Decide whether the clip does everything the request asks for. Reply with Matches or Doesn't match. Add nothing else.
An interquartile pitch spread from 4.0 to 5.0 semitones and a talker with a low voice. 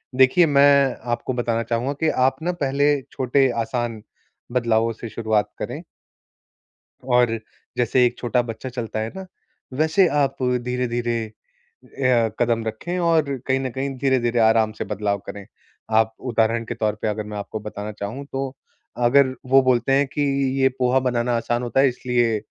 Doesn't match